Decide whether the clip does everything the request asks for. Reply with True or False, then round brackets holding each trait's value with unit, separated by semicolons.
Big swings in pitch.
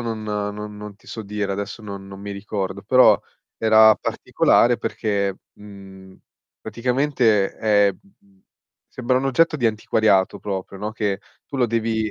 False (2.4 semitones)